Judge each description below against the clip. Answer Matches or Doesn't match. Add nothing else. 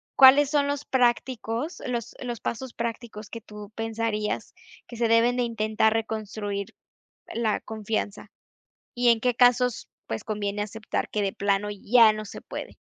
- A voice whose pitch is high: Matches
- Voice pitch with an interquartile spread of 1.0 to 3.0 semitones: Matches